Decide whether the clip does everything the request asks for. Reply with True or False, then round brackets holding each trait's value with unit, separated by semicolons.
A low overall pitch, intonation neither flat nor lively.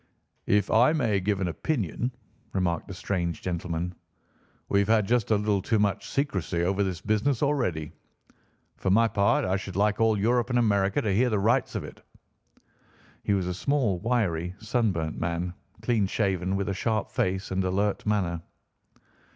True (100 Hz; 3.4 semitones)